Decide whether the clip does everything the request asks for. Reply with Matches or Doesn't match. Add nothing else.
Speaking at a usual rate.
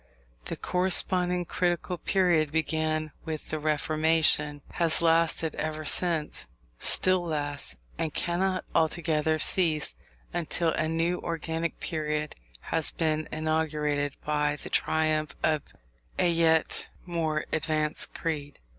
Doesn't match